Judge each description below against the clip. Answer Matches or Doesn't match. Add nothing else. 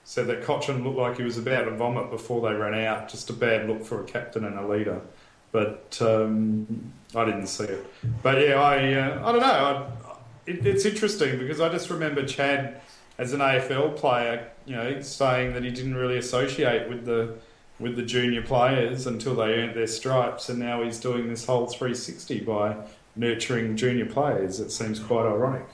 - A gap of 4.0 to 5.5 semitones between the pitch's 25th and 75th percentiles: Doesn't match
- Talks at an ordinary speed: Matches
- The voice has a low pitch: Matches